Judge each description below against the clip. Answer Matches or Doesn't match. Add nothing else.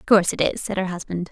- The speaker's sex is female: Matches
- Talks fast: Matches